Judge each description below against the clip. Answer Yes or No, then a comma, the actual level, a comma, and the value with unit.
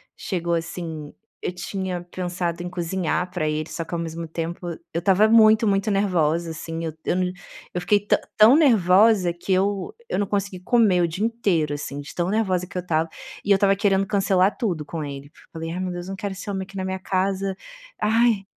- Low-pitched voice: No, medium, 185 Hz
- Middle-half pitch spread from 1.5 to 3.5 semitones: Yes, average, 2.8 semitones